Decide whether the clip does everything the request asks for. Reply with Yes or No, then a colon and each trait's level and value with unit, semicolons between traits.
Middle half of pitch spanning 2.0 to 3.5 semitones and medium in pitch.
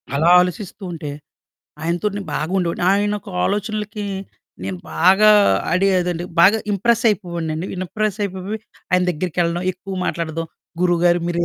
Yes: average, 3.2 semitones; medium, 180 Hz